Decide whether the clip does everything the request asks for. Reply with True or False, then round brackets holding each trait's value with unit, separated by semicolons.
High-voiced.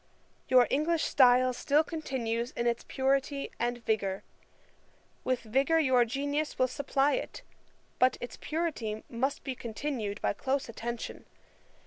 True (255 Hz)